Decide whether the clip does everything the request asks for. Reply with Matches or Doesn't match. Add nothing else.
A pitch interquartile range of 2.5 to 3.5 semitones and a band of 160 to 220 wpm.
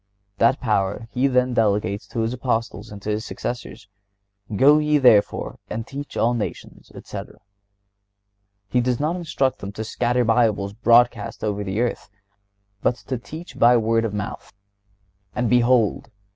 Doesn't match